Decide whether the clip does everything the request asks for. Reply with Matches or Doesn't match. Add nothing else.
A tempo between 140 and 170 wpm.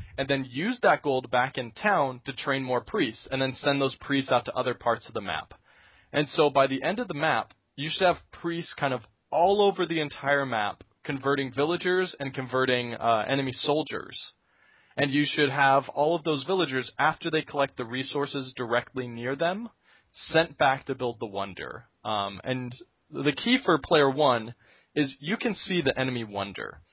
Doesn't match